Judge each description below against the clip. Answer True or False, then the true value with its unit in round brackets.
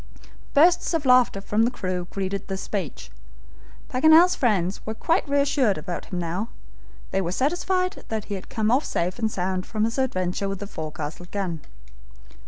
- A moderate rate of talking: True (170 wpm)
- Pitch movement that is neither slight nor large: False (6.1 semitones)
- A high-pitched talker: True (205 Hz)